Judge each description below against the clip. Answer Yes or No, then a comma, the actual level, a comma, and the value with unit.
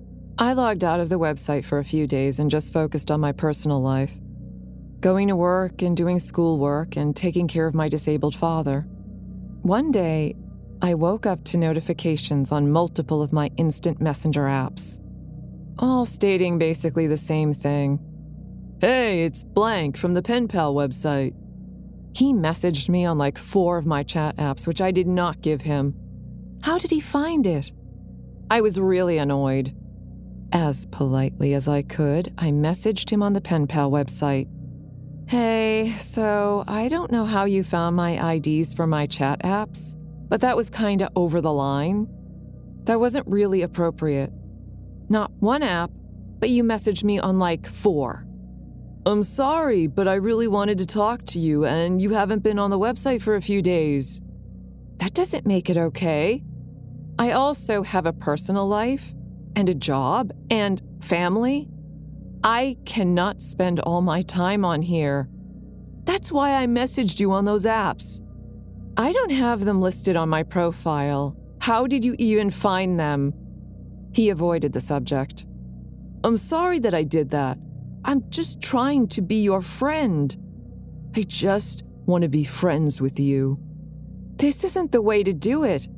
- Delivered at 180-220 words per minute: No, average, 160 wpm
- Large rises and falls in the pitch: Yes, wide, 5.7 semitones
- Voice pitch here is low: No, medium, 170 Hz